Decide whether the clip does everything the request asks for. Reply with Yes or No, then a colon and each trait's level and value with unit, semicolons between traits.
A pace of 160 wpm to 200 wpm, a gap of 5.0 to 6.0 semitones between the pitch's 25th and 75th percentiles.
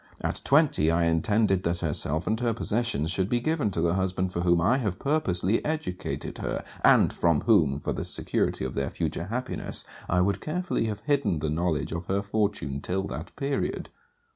Yes: average, 190 wpm; wide, 5.5 semitones